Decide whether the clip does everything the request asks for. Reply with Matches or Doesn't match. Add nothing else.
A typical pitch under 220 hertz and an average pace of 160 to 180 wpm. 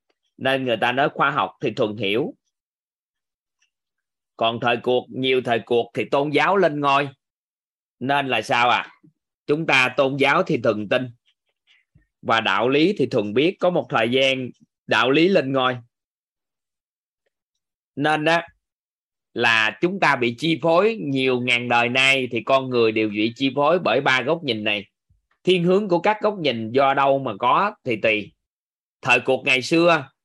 Matches